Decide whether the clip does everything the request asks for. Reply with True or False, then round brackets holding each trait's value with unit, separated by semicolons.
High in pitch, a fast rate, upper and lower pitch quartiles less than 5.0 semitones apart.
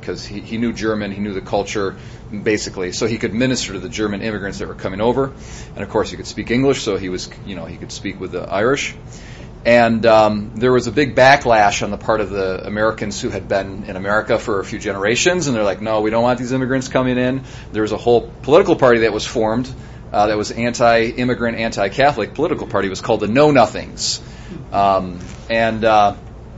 False (110 Hz; 220 wpm; 3.0 semitones)